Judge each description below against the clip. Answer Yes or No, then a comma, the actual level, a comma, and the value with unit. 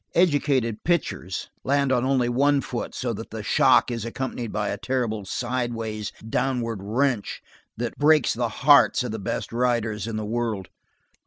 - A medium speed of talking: Yes, average, 160 wpm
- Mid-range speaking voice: No, low, 120 Hz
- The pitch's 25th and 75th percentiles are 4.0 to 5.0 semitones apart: No, average, 3.3 semitones